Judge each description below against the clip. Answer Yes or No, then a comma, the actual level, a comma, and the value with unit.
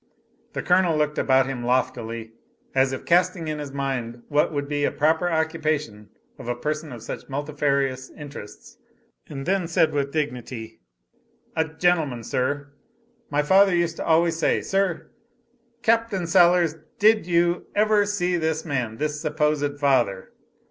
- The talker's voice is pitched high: No, medium, 150 Hz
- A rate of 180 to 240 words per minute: No, average, 150 wpm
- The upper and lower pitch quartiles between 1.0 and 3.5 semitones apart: No, average, 4.1 semitones